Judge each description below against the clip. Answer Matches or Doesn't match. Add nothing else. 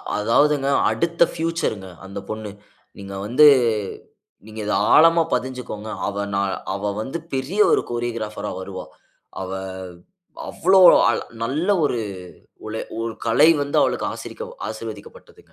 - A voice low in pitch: Matches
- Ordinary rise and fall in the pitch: Doesn't match